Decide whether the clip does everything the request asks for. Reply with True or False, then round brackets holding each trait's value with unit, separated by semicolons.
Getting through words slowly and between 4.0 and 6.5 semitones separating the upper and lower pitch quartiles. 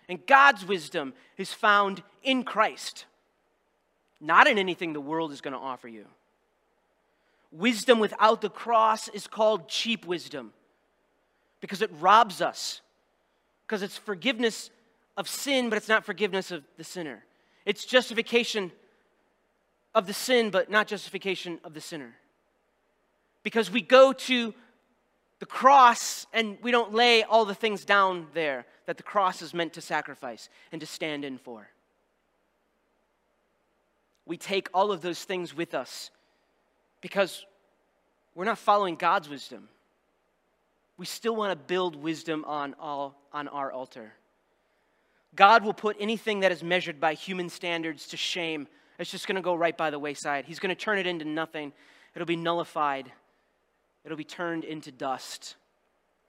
False (150 wpm; 4.9 semitones)